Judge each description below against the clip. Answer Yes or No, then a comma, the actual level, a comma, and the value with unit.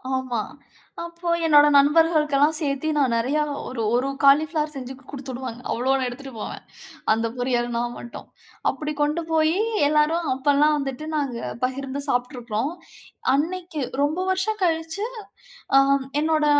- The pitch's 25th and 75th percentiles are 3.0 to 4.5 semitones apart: Yes, average, 3.4 semitones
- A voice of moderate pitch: No, very high, 285 Hz